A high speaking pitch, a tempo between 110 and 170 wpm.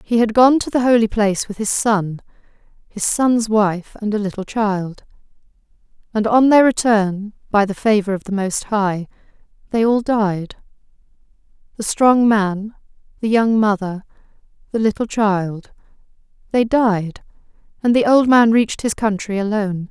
Yes: high, 215 Hz; average, 150 wpm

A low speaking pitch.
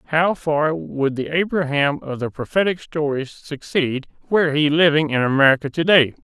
No: medium, 150 Hz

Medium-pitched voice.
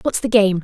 No: high, 200 Hz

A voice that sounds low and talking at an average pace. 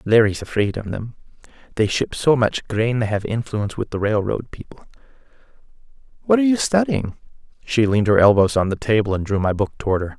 Yes: low, 110 Hz; average, 195 wpm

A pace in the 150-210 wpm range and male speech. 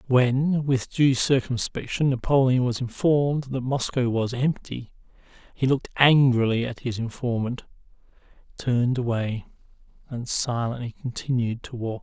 No: slow, 135 wpm; male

